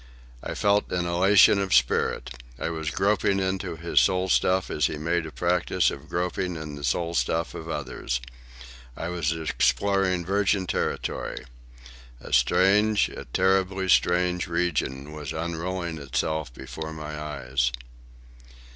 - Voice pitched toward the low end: Yes, very low, 85 Hz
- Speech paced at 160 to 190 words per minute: No, average, 140 wpm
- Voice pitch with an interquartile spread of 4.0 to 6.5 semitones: No, average, 3.6 semitones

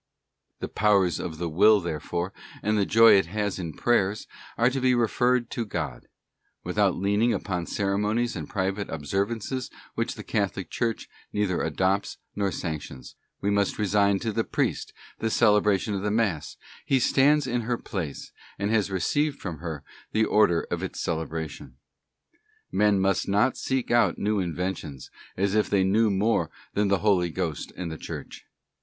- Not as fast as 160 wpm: No, average, 165 wpm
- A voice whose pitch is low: Yes, low, 100 Hz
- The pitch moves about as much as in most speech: Yes, average, 3.7 semitones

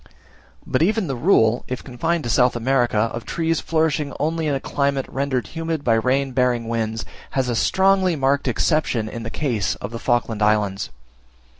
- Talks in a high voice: No, low, 130 Hz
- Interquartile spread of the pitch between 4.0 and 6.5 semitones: Yes, average, 5.1 semitones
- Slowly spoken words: No, average, 175 wpm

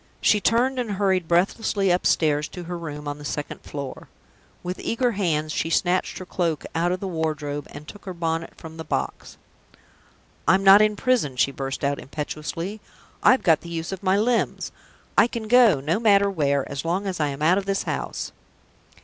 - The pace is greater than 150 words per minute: Yes, average, 190 wpm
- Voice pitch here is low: No, medium, 175 Hz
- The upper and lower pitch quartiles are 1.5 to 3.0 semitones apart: No, average, 4.8 semitones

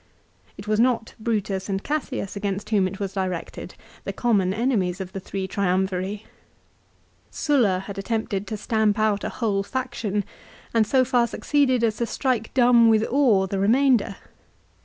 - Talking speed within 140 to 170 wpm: Yes, average, 160 wpm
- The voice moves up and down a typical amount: Yes, average, 3.5 semitones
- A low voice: No, high, 210 Hz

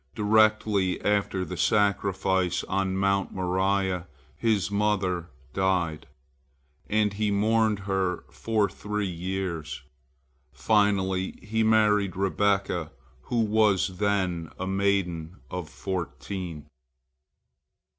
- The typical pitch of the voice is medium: No, very low, 95 Hz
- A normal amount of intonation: No, narrow, 2.2 semitones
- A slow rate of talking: Yes, slow, 95 wpm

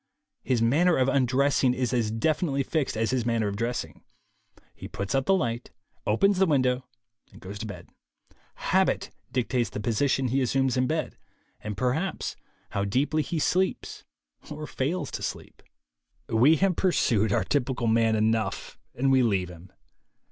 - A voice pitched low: Yes, low, 125 Hz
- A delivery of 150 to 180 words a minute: Yes, average, 160 wpm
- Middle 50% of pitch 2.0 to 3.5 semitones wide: No, average, 4.2 semitones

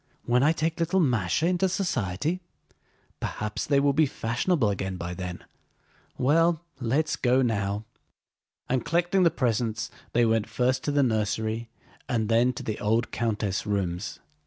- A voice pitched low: Yes, low, 120 Hz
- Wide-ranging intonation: Yes, wide, 6.1 semitones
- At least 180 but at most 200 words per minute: No, average, 150 wpm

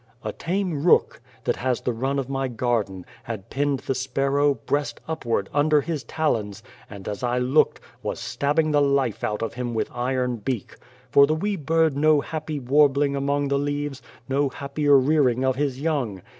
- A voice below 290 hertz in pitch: Yes, medium, 140 Hz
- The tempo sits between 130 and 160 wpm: No, average, 180 wpm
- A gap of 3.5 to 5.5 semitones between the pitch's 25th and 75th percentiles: No, average, 2.8 semitones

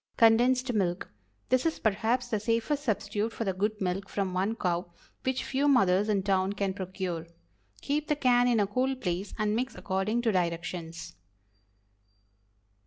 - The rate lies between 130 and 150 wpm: No, average, 160 wpm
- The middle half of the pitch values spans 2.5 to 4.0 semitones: No, average, 4.6 semitones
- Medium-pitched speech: No, high, 210 Hz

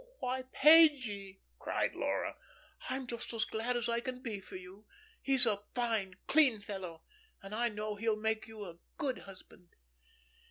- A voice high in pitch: Yes, high, 220 Hz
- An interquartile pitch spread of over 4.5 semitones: No, average, 3.9 semitones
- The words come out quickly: No, average, 165 wpm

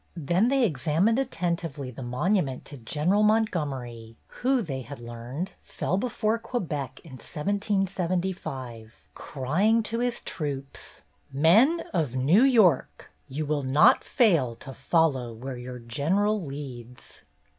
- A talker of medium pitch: Yes, medium, 150 Hz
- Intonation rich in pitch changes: Yes, wide, 7.4 semitones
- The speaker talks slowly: Yes, slow, 125 wpm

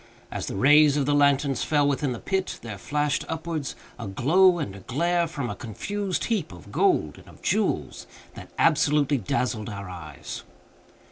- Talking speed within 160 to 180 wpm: Yes, average, 175 wpm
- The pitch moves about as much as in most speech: No, wide, 6.1 semitones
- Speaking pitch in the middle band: Yes, medium, 145 Hz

